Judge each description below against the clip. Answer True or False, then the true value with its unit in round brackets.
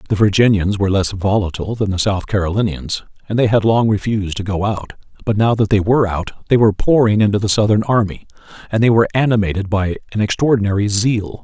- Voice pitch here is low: True (105 Hz)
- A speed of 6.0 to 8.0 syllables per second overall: True (6.4 syllables/s)